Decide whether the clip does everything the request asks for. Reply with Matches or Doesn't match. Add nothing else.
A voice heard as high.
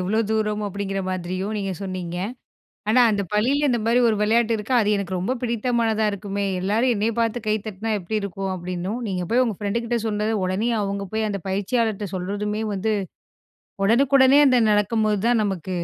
Matches